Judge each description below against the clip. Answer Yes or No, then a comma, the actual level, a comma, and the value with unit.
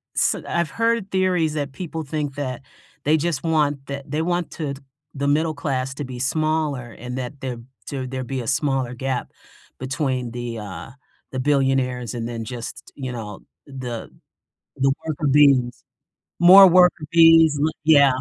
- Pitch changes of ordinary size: Yes, average, 3.5 semitones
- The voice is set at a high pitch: No, medium, 140 Hz